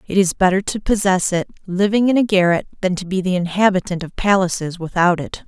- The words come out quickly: Yes, fast, 210 wpm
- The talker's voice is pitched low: No, medium, 185 Hz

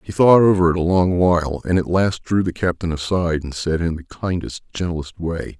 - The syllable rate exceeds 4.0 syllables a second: Yes, 5.3 syllables/s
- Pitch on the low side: Yes, very low, 85 Hz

